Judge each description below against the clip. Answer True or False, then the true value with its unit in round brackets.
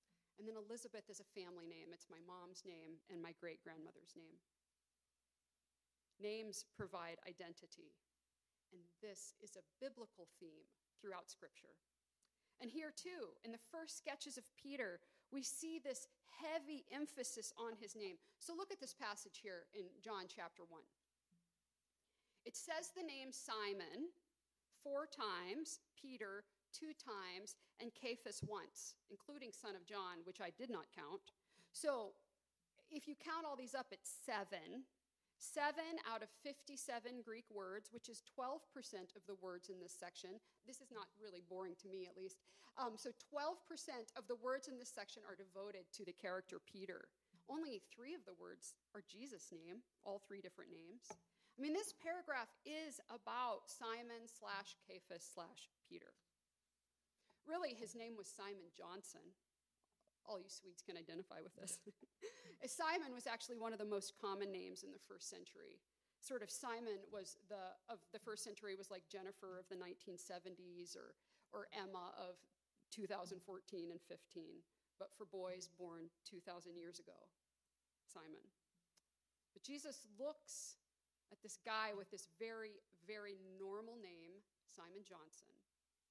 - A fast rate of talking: False (150 wpm)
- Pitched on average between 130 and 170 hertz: False (205 Hz)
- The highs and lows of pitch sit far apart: True (6.1 semitones)